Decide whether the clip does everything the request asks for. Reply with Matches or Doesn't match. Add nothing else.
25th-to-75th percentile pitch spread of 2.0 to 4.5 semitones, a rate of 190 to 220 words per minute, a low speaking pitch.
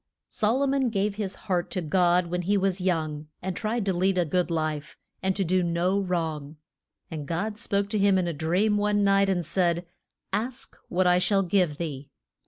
Doesn't match